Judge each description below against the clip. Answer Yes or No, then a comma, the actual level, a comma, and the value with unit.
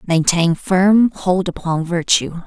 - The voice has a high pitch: No, medium, 180 Hz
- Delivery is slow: Yes, slow, 120 wpm